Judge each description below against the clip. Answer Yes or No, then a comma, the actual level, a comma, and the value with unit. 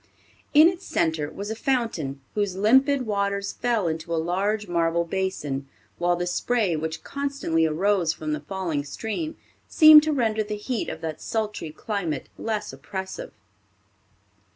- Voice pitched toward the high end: Yes, high, 195 Hz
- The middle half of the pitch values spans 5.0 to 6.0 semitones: Yes, wide, 5.4 semitones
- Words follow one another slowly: No, average, 150 wpm